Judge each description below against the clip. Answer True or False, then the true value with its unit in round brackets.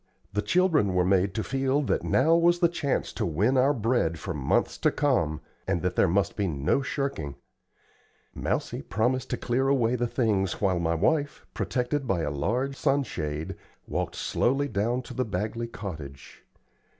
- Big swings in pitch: True (6.9 semitones)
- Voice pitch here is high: False (115 Hz)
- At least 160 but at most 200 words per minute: True (175 wpm)